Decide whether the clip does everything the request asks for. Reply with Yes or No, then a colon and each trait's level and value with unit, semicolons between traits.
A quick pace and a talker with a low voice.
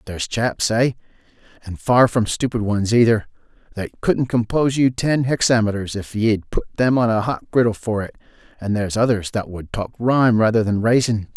No: average, 190 wpm; low, 110 Hz